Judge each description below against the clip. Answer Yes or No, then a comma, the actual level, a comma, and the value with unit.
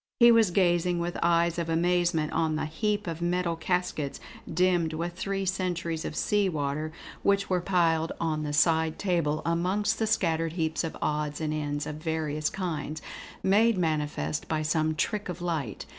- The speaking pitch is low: No, medium, 170 Hz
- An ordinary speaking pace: Yes, average, 170 wpm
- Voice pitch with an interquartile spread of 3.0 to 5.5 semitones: No, narrow, 2.5 semitones